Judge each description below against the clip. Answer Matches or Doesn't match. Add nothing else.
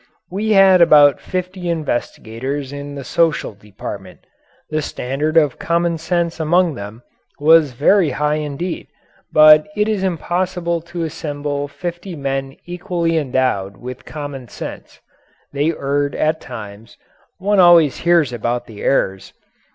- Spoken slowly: Matches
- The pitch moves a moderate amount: Matches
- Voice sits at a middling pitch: Matches